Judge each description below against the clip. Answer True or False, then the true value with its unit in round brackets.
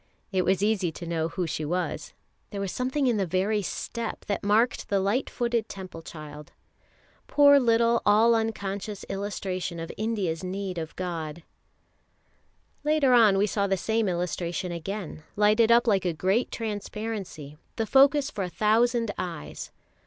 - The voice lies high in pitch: True (200 Hz)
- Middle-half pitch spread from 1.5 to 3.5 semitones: False (4.0 semitones)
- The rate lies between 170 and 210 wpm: False (155 wpm)